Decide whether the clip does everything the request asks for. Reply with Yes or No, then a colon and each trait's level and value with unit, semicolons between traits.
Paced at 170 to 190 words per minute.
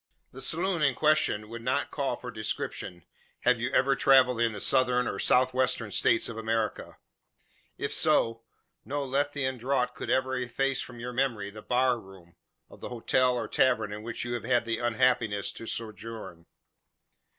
Yes: average, 175 wpm